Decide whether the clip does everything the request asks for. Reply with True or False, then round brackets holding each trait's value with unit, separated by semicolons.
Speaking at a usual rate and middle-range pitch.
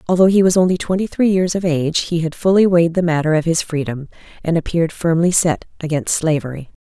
False (210 wpm; 170 Hz)